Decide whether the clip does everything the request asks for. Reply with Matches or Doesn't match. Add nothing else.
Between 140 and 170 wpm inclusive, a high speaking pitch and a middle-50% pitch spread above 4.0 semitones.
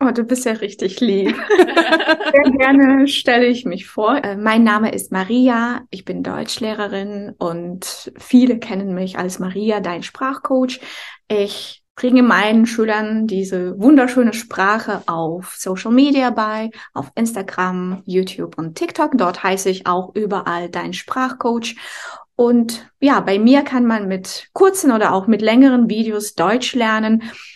Matches